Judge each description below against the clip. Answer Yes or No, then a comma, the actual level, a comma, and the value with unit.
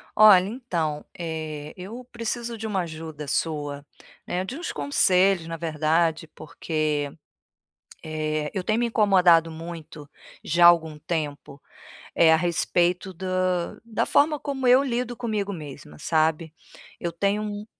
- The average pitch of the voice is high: No, medium, 170 Hz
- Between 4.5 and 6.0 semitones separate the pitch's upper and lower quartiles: Yes, average, 4.8 semitones